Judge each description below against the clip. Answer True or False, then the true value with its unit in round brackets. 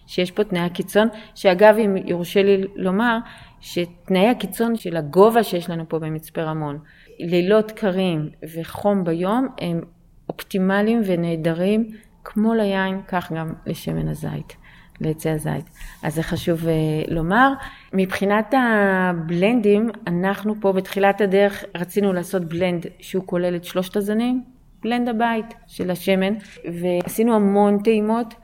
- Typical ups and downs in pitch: True (3.6 semitones)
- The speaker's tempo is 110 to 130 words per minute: True (120 wpm)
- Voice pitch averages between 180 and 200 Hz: True (190 Hz)